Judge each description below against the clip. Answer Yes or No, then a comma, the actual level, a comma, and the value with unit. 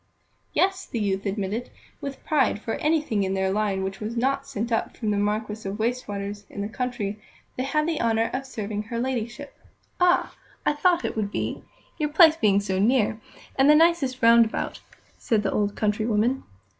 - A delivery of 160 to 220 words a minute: Yes, average, 195 wpm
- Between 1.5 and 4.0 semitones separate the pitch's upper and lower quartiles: No, average, 4.7 semitones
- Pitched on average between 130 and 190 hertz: No, high, 225 Hz